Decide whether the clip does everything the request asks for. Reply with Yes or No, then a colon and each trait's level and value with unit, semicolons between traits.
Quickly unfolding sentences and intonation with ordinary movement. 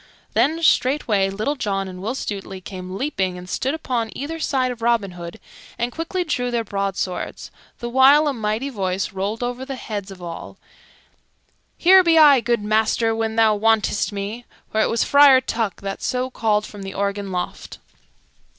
No: average, 175 wpm; average, 4.8 semitones